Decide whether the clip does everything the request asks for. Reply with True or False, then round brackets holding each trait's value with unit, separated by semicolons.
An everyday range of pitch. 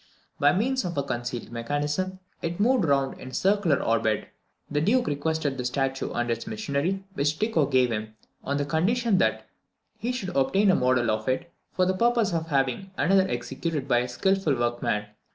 False (6.9 semitones)